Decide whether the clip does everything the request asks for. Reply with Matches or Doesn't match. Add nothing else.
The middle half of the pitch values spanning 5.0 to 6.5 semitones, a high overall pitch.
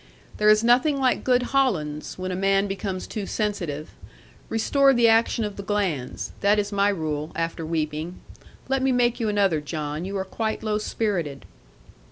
Matches